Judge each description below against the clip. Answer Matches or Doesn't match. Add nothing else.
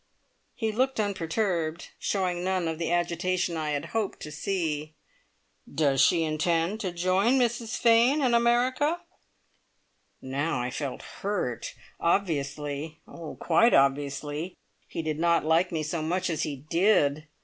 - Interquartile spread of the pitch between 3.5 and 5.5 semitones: Matches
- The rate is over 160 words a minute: Doesn't match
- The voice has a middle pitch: Matches